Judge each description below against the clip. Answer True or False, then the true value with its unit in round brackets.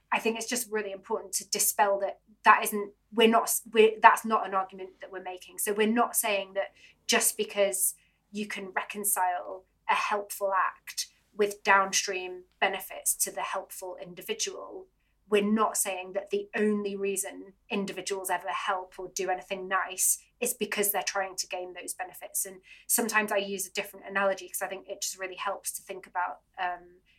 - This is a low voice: False (195 Hz)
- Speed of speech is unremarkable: True (180 wpm)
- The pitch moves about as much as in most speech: False (2.1 semitones)